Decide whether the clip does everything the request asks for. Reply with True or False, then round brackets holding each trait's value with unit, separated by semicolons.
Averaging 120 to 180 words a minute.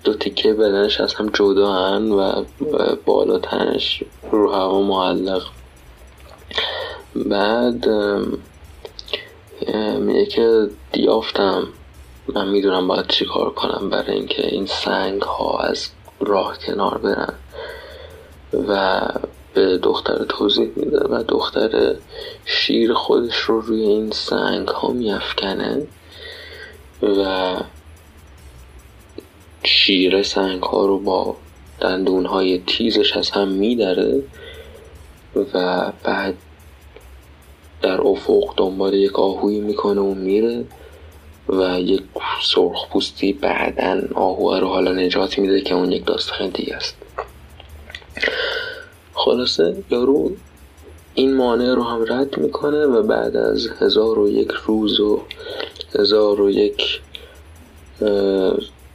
False (105 wpm)